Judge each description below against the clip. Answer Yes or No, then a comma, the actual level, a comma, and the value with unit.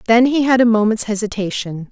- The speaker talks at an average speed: Yes, average, 190 wpm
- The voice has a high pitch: Yes, high, 225 Hz